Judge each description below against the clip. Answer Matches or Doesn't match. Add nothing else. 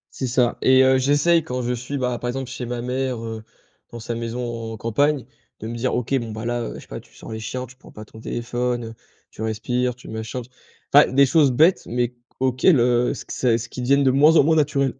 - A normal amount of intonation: Doesn't match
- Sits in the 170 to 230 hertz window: Doesn't match